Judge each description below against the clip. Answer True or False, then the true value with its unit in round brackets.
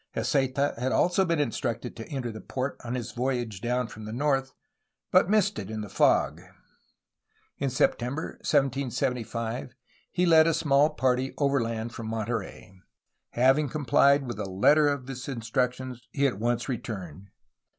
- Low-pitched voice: True (125 Hz)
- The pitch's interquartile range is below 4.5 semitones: True (3.5 semitones)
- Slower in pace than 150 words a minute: False (155 wpm)